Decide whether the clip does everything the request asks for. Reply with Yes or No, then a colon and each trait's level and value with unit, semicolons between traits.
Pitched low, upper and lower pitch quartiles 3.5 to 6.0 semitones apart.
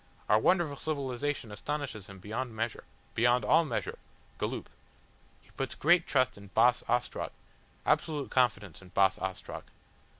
Yes: low, 120 Hz; wide, 5.6 semitones